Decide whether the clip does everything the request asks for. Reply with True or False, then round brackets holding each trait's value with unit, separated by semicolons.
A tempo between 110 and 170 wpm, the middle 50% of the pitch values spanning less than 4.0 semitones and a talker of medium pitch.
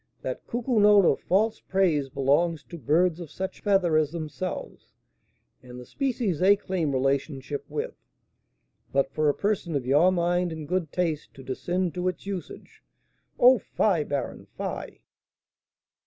False (150 wpm; 4.7 semitones; 170 Hz)